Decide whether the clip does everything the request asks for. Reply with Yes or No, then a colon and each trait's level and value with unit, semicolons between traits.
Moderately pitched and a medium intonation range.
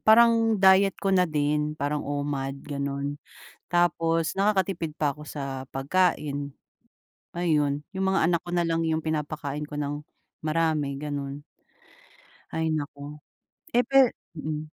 Yes: medium, 155 Hz; average, 3.3 semitones